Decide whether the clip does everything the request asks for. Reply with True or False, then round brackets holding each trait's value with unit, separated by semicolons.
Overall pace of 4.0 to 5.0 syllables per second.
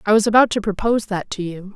False (6.8 syllables/s)